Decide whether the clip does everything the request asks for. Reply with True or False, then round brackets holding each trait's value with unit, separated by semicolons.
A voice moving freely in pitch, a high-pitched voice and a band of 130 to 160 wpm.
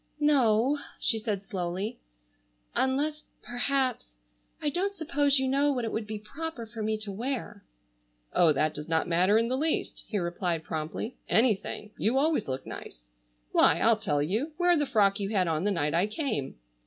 False (7.5 semitones; 215 Hz; 175 wpm)